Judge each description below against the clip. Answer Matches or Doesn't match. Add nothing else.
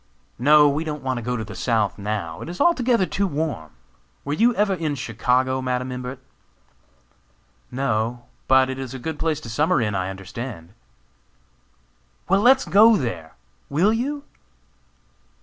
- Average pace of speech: Matches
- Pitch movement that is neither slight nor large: Doesn't match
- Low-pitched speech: Matches